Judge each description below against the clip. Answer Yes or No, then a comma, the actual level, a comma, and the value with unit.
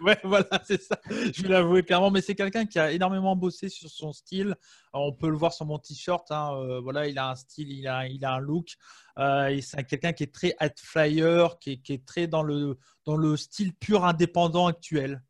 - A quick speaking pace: Yes, fast, 235 wpm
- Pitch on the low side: No, medium, 160 Hz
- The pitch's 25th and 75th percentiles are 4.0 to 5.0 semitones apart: Yes, average, 4.4 semitones